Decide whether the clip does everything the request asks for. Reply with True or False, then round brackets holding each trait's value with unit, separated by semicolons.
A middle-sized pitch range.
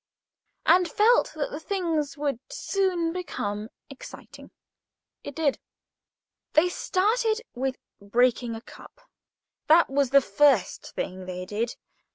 False (7.3 semitones)